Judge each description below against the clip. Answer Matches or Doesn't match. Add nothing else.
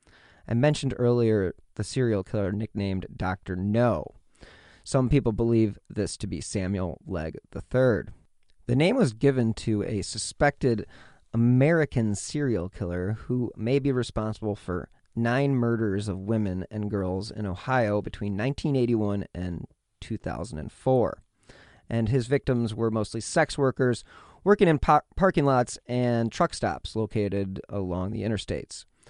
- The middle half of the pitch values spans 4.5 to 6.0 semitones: Doesn't match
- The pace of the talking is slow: Matches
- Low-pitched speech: Matches